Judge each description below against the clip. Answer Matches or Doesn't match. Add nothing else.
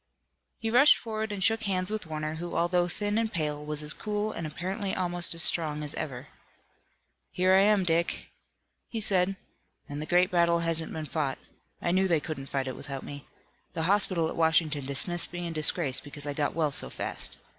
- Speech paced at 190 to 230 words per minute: Matches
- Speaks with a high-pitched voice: Doesn't match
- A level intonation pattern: Doesn't match